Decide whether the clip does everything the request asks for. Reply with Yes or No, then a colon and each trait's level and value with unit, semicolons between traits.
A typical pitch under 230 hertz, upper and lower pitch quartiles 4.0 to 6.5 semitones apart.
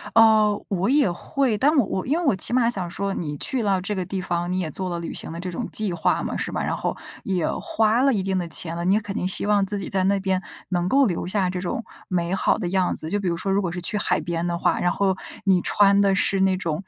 No: high, 190 Hz; average, 2.7 semitones